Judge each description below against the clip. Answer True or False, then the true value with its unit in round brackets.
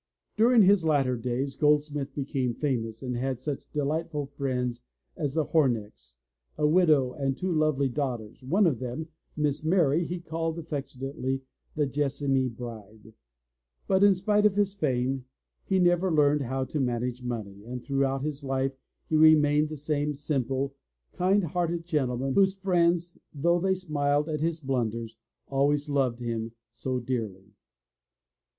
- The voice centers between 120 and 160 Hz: True (140 Hz)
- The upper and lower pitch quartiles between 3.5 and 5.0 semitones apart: True (4.0 semitones)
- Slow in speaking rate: False (150 wpm)